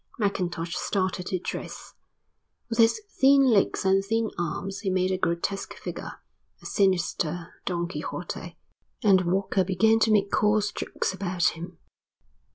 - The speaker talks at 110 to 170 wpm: Yes, average, 140 wpm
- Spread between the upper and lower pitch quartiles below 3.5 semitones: Yes, average, 2.7 semitones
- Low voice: No, high, 190 Hz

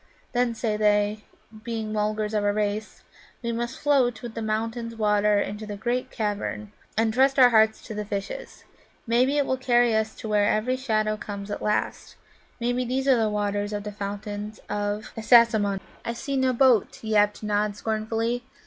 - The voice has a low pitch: No, high, 220 Hz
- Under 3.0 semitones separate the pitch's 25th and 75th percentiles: Yes, narrow, 2.4 semitones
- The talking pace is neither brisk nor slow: Yes, average, 175 wpm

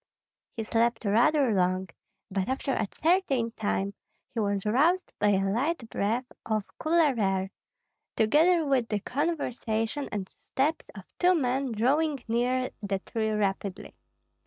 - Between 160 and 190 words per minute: No, slow, 135 wpm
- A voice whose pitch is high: Yes, high, 230 Hz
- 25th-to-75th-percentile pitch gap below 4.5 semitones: No, wide, 5.4 semitones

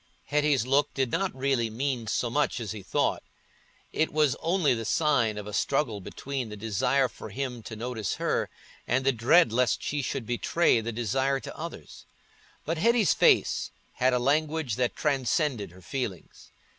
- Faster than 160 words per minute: Yes, average, 170 wpm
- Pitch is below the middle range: Yes, low, 130 Hz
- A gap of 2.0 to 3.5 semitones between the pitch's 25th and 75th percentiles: No, average, 4.2 semitones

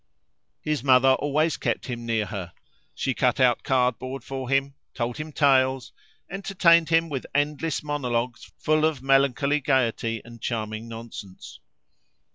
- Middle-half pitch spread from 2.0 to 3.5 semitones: No, average, 3.9 semitones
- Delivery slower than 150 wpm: Yes, slow, 135 wpm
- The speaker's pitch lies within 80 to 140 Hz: Yes, low, 135 Hz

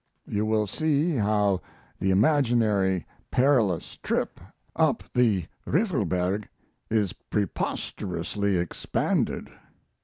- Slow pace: Yes, slow, 85 wpm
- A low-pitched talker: Yes, low, 105 Hz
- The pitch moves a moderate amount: Yes, average, 4.5 semitones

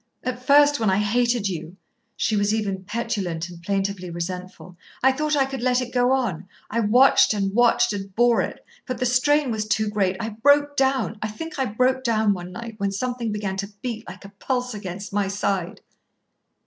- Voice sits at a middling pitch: No, high, 220 Hz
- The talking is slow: No, average, 200 wpm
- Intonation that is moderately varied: Yes, average, 4.3 semitones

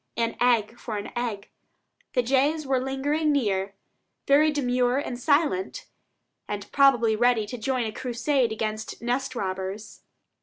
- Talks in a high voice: Yes, high, 245 Hz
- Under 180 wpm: Yes, average, 140 wpm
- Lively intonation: No, average, 3.8 semitones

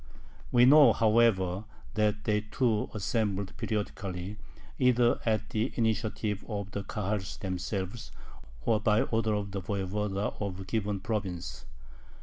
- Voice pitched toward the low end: Yes, low, 105 Hz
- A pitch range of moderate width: No, narrow, 2.3 semitones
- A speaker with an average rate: No, slow, 130 wpm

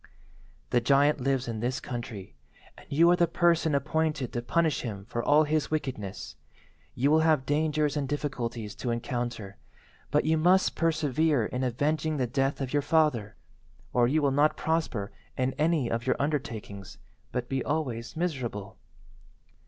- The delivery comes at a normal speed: Yes, average, 160 wpm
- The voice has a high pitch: No, medium, 140 Hz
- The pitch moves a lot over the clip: No, average, 4.5 semitones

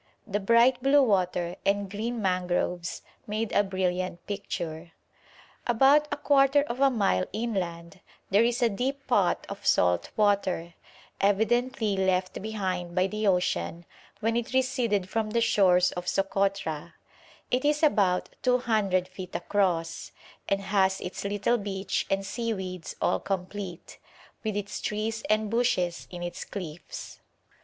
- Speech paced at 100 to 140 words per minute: Yes, slow, 135 wpm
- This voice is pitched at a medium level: No, high, 200 Hz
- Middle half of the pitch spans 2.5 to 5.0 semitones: Yes, average, 3.9 semitones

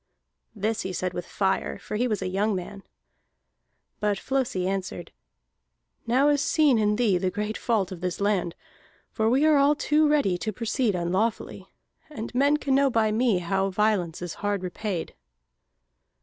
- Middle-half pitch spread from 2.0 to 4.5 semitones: No, average, 4.9 semitones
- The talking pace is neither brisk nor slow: Yes, average, 165 wpm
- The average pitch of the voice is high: Yes, high, 210 Hz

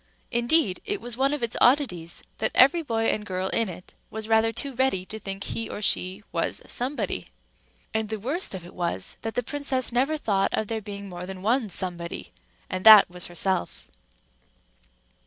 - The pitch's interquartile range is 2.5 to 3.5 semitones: No, average, 4.9 semitones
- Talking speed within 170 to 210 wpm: Yes, average, 180 wpm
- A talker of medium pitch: No, high, 220 Hz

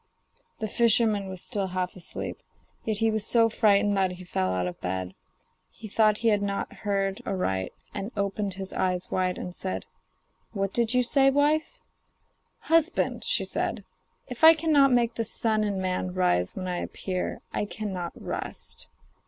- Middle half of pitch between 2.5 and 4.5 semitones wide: Yes, average, 3.7 semitones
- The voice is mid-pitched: No, high, 200 Hz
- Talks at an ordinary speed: Yes, average, 170 wpm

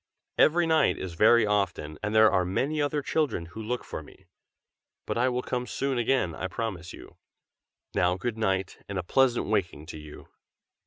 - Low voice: Yes, low, 110 Hz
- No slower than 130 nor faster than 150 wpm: No, average, 180 wpm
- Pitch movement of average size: No, wide, 5.7 semitones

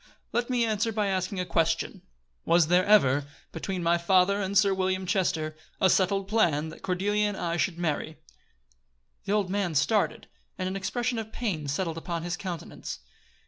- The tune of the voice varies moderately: Yes, average, 3.3 semitones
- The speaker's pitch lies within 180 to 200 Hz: Yes, medium, 185 Hz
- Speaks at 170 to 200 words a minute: Yes, average, 175 wpm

